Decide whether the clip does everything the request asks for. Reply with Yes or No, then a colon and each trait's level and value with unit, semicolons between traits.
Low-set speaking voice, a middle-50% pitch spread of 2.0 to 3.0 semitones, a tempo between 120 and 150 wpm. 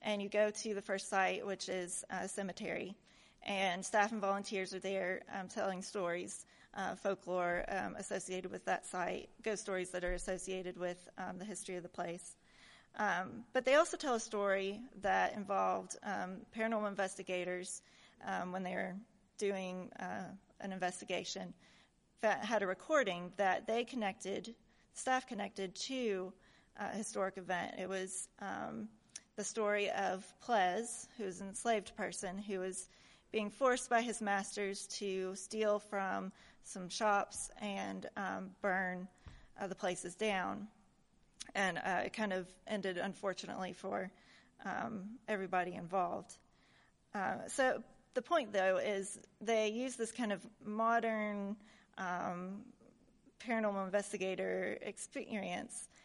No: high, 195 Hz; narrow, 2.5 semitones; average, 140 wpm